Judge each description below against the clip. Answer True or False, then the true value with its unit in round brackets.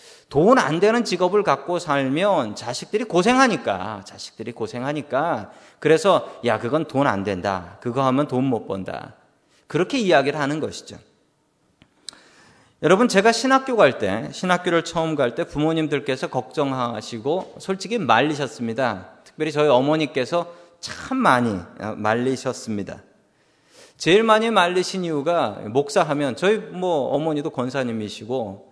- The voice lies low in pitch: False (145 Hz)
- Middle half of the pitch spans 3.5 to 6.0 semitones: False (6.6 semitones)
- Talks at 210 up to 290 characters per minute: False (300 characters per minute)